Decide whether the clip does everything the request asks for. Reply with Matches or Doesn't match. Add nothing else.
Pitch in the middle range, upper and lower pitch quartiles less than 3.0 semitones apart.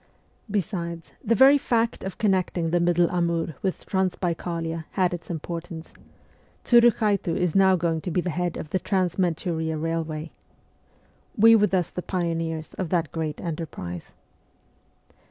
Matches